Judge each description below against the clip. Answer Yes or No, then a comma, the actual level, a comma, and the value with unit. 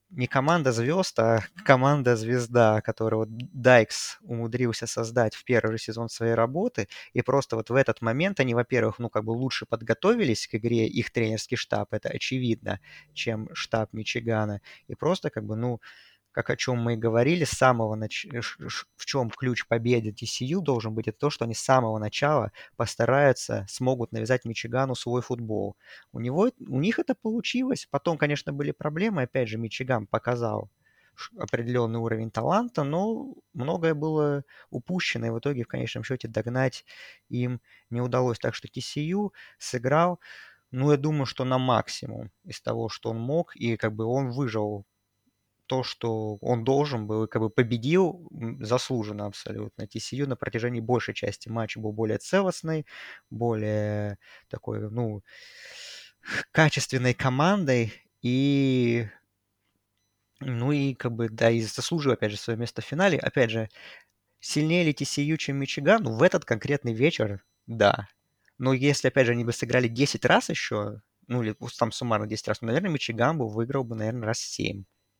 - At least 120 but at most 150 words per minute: No, fast, 160 wpm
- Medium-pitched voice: No, low, 120 Hz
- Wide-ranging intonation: No, average, 3.8 semitones